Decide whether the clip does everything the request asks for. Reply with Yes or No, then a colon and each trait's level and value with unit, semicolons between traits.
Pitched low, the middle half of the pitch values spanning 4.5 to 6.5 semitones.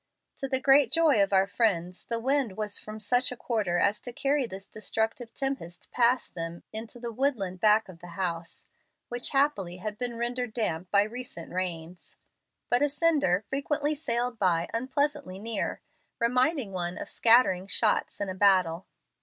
No: high, 220 Hz; average, 5.3 semitones